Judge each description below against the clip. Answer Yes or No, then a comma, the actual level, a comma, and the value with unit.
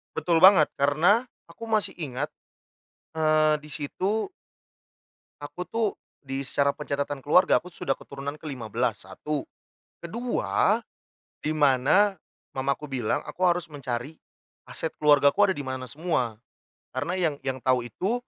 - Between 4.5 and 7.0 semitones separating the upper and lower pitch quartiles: Yes, average, 5.1 semitones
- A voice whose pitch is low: No, medium, 150 Hz